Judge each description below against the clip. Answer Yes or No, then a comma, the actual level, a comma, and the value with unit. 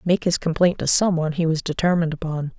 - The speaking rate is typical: No, fast, 230 wpm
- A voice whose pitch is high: No, medium, 165 Hz